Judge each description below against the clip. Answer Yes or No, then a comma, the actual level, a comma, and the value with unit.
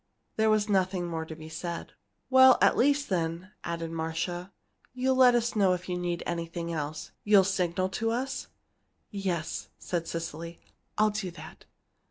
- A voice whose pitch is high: No, medium, 180 Hz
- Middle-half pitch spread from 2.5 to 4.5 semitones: Yes, average, 4.2 semitones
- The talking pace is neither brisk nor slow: Yes, average, 155 wpm